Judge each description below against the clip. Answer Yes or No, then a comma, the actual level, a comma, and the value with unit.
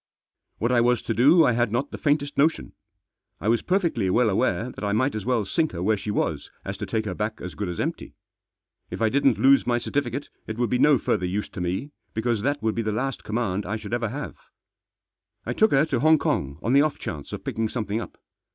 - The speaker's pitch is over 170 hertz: No, low, 115 Hz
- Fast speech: Yes, fast, 245 wpm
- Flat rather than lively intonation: No, average, 4.6 semitones